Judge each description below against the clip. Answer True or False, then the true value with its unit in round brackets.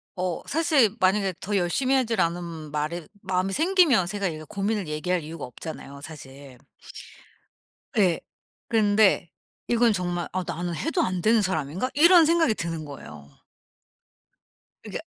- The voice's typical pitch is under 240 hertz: True (185 Hz)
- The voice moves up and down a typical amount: False (5.7 semitones)